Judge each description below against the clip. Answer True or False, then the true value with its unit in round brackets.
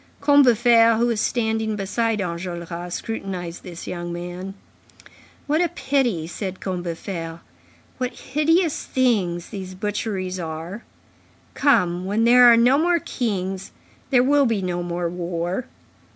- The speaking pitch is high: True (200 Hz)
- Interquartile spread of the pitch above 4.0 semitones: True (5.6 semitones)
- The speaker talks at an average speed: False (125 wpm)